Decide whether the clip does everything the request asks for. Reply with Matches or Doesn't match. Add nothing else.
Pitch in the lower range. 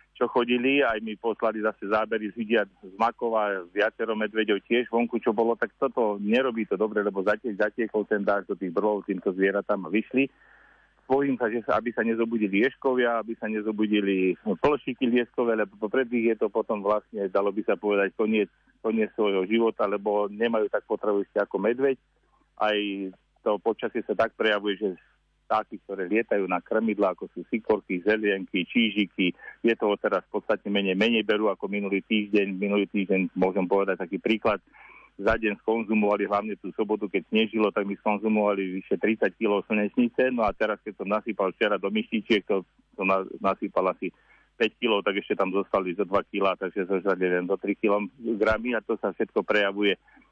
Matches